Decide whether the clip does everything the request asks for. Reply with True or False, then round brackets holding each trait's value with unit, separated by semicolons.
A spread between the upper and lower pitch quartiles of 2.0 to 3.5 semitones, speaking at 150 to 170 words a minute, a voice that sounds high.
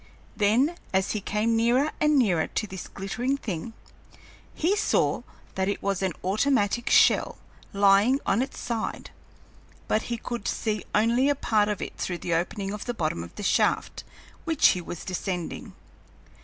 False (4.0 semitones; 165 wpm; 210 Hz)